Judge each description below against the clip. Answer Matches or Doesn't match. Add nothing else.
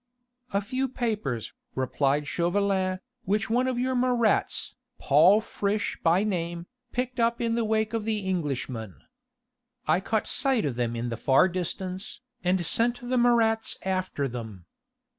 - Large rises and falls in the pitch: Matches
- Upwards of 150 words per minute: Doesn't match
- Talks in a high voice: Matches